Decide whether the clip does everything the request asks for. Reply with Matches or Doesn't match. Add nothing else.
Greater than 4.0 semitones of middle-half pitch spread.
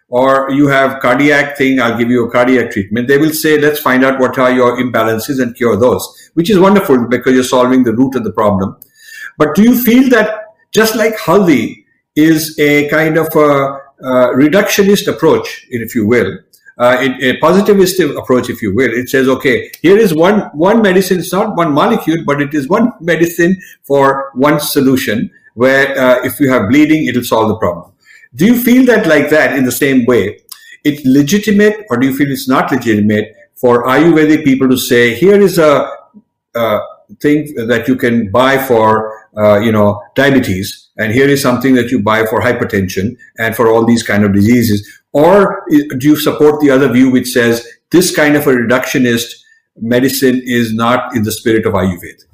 Matches